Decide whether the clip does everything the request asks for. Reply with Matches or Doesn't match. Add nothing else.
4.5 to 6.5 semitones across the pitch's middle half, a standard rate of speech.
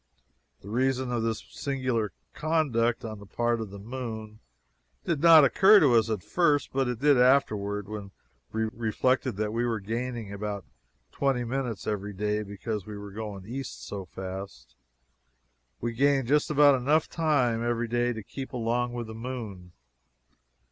Doesn't match